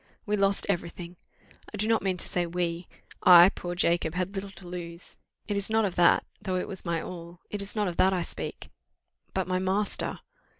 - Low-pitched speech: No, medium, 185 Hz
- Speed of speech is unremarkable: No, fast, 215 wpm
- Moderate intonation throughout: No, narrow, 2.3 semitones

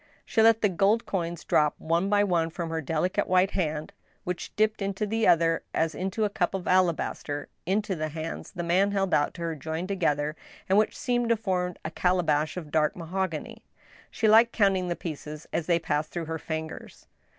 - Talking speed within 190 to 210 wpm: Yes, average, 195 wpm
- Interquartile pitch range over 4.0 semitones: No, average, 3.6 semitones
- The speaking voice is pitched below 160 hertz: No, medium, 180 Hz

